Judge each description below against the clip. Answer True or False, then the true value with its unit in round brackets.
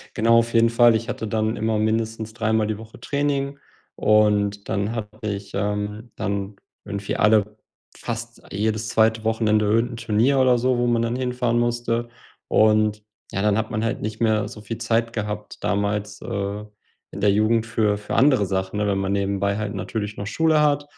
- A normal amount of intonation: False (2.0 semitones)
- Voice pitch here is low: True (110 Hz)